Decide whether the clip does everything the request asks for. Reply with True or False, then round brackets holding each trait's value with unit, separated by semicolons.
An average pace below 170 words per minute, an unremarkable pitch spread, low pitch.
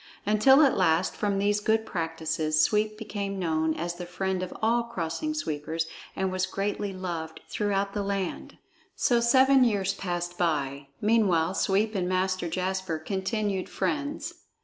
False (150 wpm; 3.6 semitones; 190 Hz)